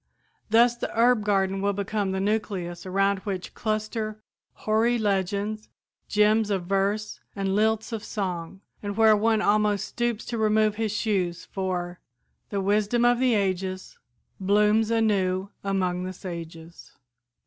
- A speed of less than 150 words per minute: Yes, slow, 135 wpm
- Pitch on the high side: Yes, high, 205 Hz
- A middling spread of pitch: No, narrow, 2.2 semitones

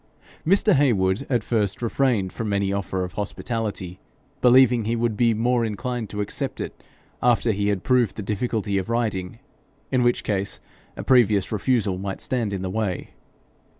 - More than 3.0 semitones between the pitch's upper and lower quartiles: Yes, average, 3.5 semitones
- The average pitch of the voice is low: Yes, low, 110 Hz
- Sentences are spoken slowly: No, average, 165 wpm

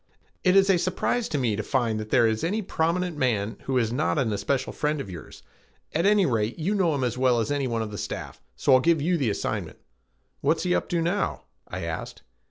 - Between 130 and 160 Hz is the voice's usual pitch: Yes, medium, 140 Hz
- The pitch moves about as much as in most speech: No, wide, 7.1 semitones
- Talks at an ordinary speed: No, fast, 230 wpm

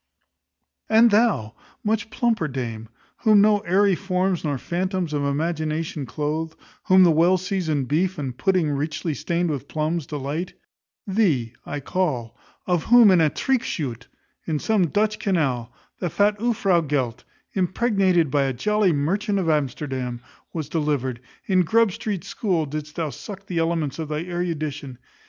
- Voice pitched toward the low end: No, medium, 165 Hz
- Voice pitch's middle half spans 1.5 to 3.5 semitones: No, average, 4.9 semitones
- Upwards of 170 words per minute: No, average, 150 wpm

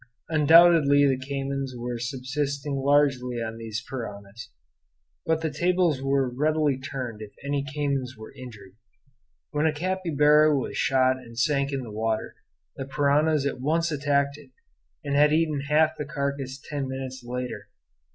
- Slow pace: No, average, 150 wpm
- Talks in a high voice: No, medium, 140 Hz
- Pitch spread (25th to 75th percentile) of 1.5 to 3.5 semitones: Yes, average, 2.7 semitones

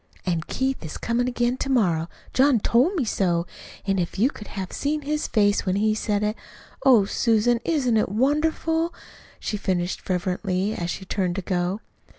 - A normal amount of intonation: No, wide, 5.7 semitones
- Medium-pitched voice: No, high, 215 Hz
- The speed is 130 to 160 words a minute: No, average, 175 wpm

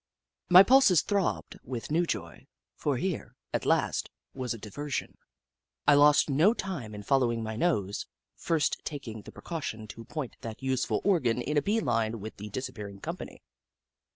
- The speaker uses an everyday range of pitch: No, wide, 6.5 semitones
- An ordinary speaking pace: Yes, average, 165 wpm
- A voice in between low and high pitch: No, low, 130 Hz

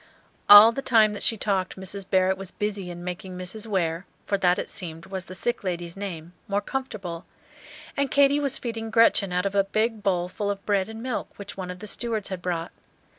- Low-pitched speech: No, high, 195 Hz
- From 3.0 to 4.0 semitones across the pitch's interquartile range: Yes, average, 3.3 semitones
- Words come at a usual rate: No, fast, 215 wpm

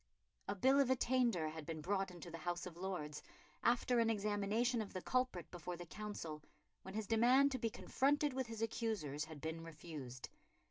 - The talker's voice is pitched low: No, high, 200 Hz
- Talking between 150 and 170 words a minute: No, average, 185 wpm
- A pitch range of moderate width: No, wide, 6.4 semitones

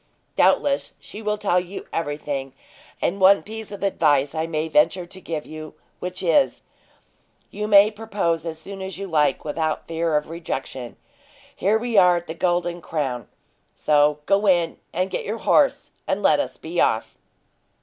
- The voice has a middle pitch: Yes, medium, 175 Hz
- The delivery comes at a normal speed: Yes, average, 170 wpm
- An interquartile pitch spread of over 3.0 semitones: Yes, average, 4.2 semitones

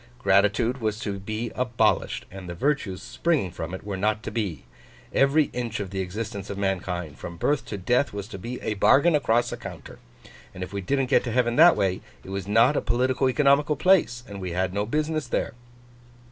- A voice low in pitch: Yes, low, 110 Hz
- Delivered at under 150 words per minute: No, fast, 205 wpm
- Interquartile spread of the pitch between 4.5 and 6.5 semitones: Yes, average, 5.1 semitones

